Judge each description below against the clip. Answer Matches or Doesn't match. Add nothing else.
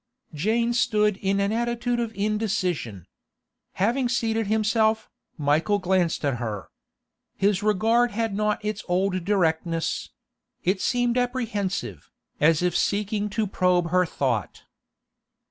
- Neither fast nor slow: Doesn't match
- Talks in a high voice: Matches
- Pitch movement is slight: Doesn't match